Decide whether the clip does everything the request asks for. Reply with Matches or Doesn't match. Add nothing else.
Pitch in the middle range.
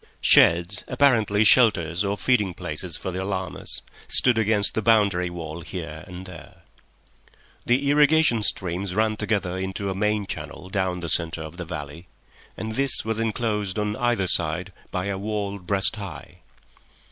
Doesn't match